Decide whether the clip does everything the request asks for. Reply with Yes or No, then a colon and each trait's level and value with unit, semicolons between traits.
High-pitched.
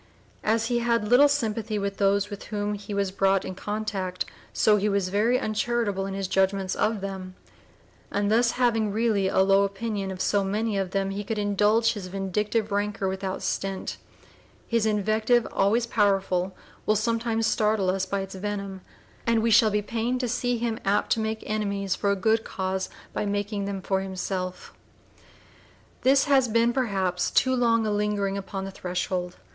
Yes: high, 205 Hz